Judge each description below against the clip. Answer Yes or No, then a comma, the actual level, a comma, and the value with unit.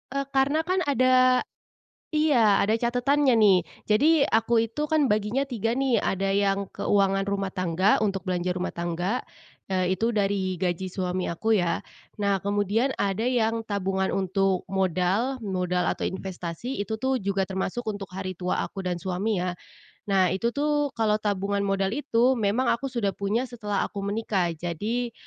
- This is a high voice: Yes, high, 200 Hz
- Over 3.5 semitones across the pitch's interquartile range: Yes, average, 4.0 semitones